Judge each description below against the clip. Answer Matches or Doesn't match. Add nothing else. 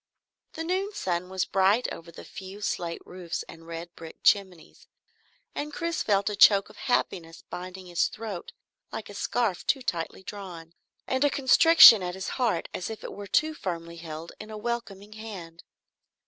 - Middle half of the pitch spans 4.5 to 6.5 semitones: Matches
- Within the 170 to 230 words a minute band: Matches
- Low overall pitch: Doesn't match